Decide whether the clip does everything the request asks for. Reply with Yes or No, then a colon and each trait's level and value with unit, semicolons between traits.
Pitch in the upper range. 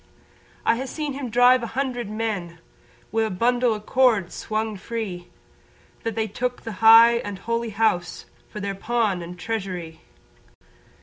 Yes: high, 225 Hz